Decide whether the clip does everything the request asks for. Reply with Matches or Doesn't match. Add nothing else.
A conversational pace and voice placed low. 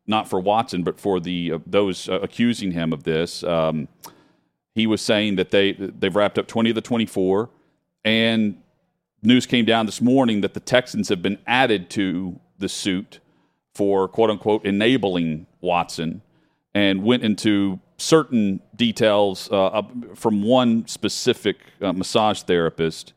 Matches